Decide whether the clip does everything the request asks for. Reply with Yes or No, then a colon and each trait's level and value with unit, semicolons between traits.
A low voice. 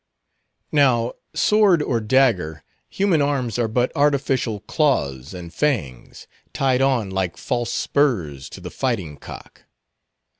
Yes: low, 120 Hz